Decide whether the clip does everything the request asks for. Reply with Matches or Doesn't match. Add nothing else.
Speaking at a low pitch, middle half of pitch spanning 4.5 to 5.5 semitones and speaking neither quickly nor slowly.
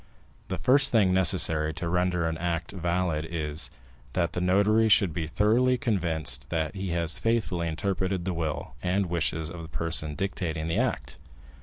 Doesn't match